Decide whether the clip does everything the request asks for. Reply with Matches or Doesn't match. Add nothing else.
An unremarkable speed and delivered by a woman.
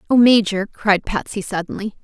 Matches